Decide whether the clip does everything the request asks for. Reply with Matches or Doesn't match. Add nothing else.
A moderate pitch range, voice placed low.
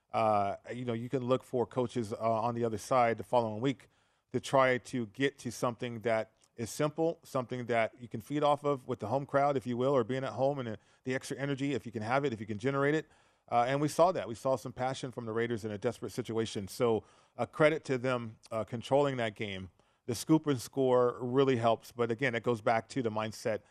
Matches